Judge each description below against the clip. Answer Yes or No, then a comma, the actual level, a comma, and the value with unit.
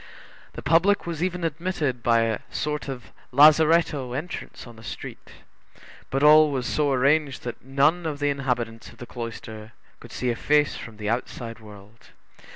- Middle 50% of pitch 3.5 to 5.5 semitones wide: Yes, average, 4.6 semitones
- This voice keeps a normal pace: Yes, average, 165 wpm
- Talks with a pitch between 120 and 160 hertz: Yes, low, 135 Hz